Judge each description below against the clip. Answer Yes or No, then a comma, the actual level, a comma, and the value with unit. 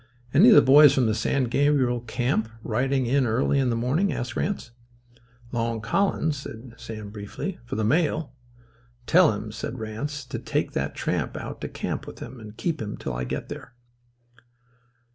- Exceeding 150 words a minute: Yes, average, 180 wpm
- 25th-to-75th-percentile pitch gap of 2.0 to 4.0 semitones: No, average, 4.4 semitones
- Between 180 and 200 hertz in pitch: No, low, 125 Hz